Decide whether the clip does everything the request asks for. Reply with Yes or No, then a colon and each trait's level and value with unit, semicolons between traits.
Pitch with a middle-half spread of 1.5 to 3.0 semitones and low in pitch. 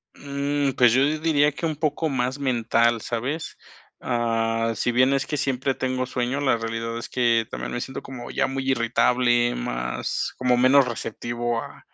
Yes: narrow, 2.6 semitones; low, 125 Hz